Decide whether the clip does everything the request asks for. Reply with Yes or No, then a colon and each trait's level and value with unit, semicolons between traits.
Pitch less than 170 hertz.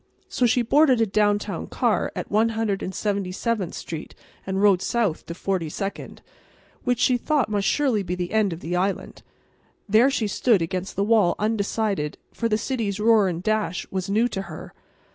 No: high, 205 Hz